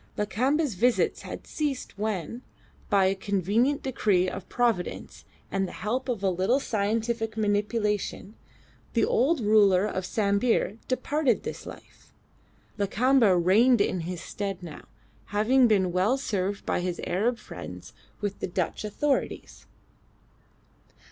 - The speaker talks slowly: Yes, slow, 130 wpm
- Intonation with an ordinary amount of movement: Yes, average, 4.0 semitones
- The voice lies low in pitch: No, high, 210 Hz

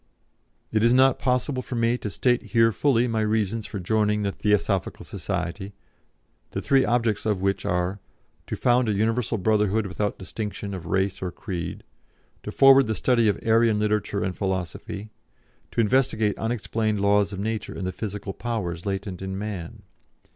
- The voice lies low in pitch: Yes, low, 105 Hz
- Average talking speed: Yes, average, 165 wpm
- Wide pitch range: No, average, 2.8 semitones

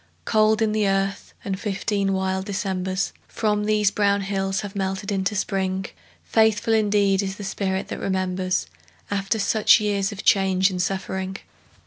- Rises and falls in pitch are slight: Yes, narrow, 1.5 semitones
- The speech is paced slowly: No, average, 150 wpm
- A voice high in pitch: Yes, high, 195 Hz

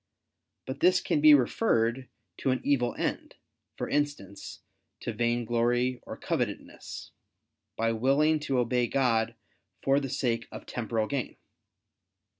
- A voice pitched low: Yes, low, 125 Hz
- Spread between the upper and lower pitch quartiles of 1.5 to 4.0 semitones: Yes, average, 3.3 semitones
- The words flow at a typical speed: No, slow, 125 wpm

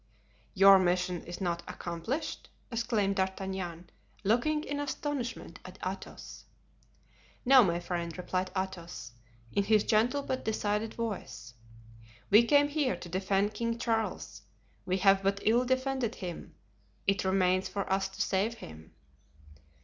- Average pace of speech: No, slow, 125 wpm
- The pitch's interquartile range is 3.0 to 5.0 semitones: Yes, average, 4.3 semitones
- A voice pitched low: No, high, 195 Hz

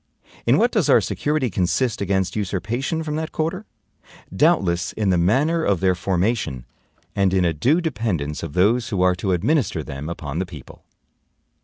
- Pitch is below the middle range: Yes, very low, 95 Hz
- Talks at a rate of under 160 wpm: No, average, 170 wpm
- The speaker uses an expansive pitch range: Yes, wide, 6.6 semitones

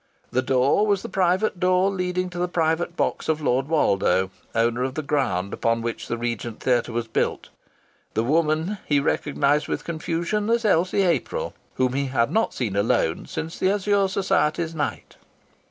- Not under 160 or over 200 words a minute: Yes, average, 170 wpm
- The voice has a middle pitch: Yes, medium, 155 Hz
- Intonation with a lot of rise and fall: Yes, wide, 6.9 semitones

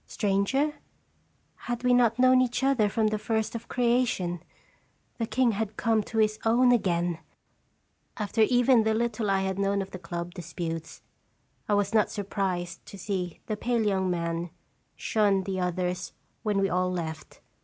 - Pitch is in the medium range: No, high, 205 Hz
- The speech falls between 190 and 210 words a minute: No, average, 165 wpm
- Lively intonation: No, average, 4.0 semitones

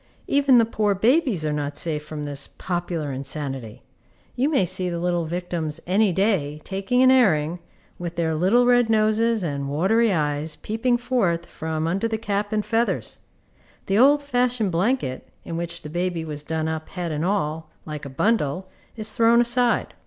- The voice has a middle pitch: Yes, medium, 180 Hz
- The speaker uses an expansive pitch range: Yes, wide, 6.4 semitones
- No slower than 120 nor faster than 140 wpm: No, average, 175 wpm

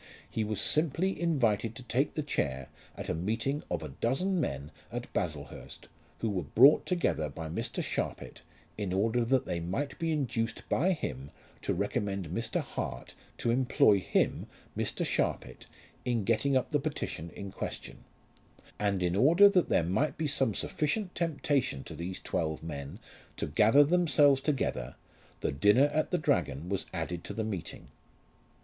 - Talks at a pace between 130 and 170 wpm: Yes, average, 160 wpm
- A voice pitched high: No, low, 115 Hz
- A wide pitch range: Yes, wide, 8.6 semitones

